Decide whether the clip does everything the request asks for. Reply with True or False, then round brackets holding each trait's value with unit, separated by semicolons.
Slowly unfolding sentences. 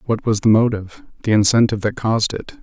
False (205 wpm)